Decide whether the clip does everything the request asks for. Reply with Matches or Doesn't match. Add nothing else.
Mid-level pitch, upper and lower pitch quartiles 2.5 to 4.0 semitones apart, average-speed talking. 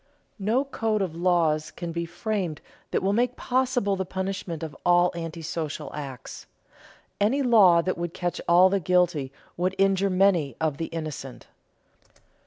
Matches